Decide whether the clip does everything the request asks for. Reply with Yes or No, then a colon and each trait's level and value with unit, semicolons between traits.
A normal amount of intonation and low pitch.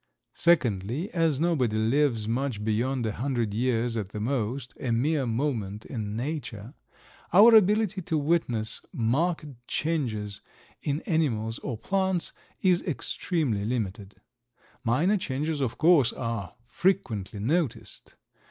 No: wide, 6.5 semitones; low, 130 Hz